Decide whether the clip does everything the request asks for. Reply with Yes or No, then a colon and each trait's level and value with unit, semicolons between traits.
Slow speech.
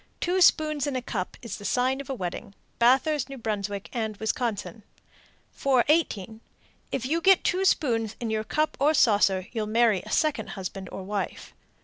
No: average, 165 wpm